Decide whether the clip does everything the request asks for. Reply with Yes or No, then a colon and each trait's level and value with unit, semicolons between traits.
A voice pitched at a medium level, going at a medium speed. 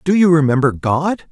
Yes: medium, 155 Hz; average, 185 wpm